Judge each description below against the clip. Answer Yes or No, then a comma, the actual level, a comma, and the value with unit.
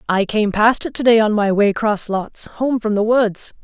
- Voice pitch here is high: Yes, high, 215 Hz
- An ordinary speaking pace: No, fast, 230 wpm